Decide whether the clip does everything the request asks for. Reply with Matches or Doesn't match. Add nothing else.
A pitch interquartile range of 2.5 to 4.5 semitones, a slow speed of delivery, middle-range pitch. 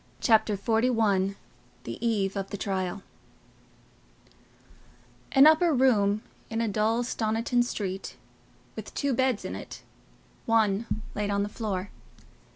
Doesn't match